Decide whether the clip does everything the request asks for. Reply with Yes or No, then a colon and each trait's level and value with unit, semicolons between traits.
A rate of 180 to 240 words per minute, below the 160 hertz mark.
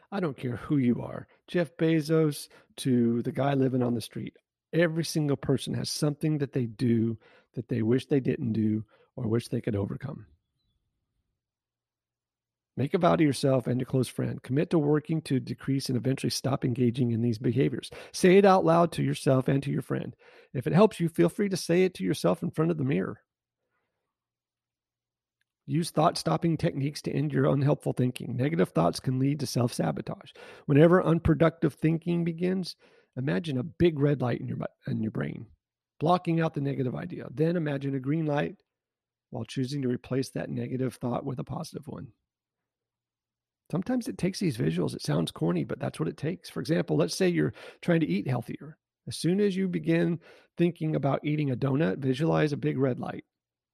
Yes: average, 190 wpm; medium, 140 Hz